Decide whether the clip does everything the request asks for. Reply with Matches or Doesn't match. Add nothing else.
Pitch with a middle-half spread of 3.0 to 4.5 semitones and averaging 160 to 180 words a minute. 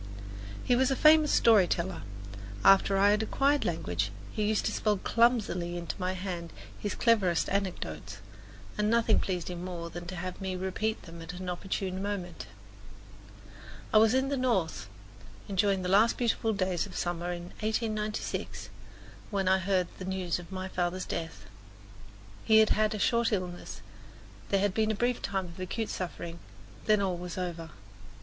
Matches